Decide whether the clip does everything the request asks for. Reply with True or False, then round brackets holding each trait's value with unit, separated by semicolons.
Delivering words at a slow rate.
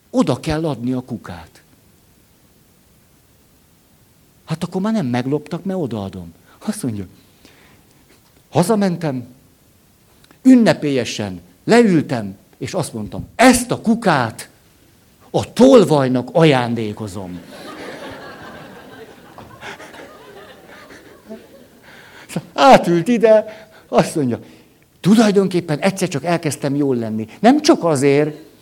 True (85 wpm)